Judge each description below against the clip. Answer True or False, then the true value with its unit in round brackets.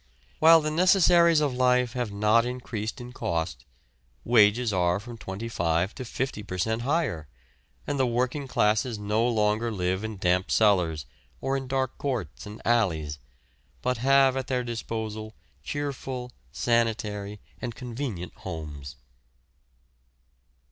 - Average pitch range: True (4.1 semitones)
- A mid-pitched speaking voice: False (115 Hz)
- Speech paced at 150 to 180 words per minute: False (135 wpm)